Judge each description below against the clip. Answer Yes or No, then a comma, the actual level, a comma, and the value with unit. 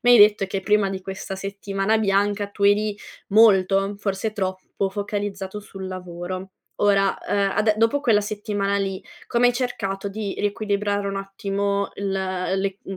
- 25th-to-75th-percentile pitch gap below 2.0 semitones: Yes, narrow, 1.2 semitones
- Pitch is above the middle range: Yes, high, 200 Hz